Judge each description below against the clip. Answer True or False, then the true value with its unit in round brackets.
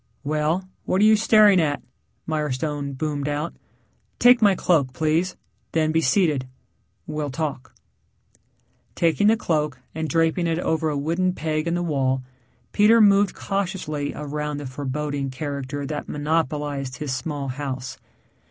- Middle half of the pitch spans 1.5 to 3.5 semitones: True (3.0 semitones)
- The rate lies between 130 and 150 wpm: True (140 wpm)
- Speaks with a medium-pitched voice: True (150 Hz)